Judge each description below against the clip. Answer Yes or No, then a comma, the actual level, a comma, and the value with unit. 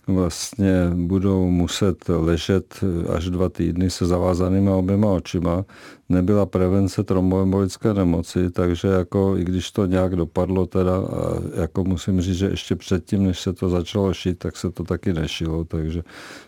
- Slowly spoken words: No, average, 150 wpm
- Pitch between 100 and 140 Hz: No, very low, 90 Hz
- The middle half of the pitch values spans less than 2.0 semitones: Yes, narrow, 1.6 semitones